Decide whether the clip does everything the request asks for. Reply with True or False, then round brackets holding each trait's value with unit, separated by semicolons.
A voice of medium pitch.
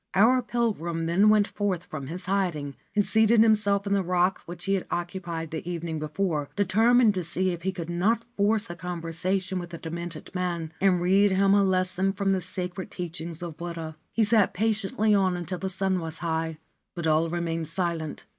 True (180 Hz)